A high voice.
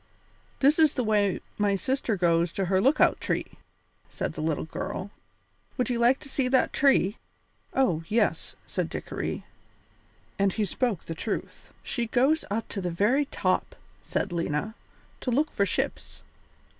Yes: high, 220 Hz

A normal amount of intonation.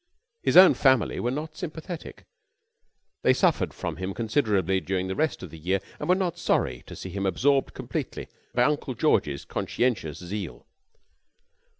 No: wide, 8.1 semitones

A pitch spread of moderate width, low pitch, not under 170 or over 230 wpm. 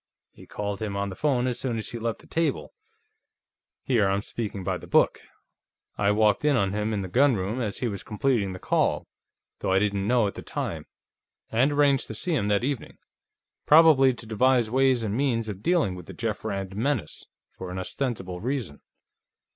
Yes: average, 4.6 semitones; low, 110 Hz; average, 200 wpm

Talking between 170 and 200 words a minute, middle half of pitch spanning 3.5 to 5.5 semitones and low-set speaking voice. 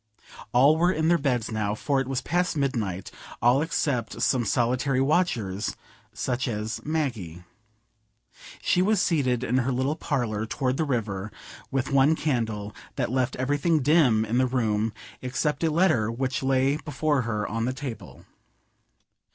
No: average, 150 wpm; average, 4.3 semitones; low, 130 Hz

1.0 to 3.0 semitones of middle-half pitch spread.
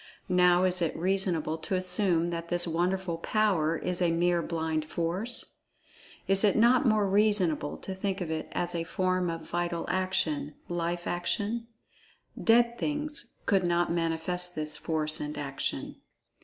Yes: narrow, 2.5 semitones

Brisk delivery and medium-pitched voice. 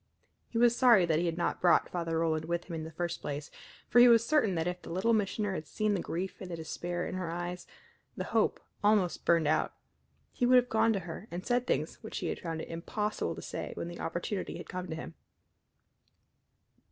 Yes: fast, 225 wpm; medium, 175 Hz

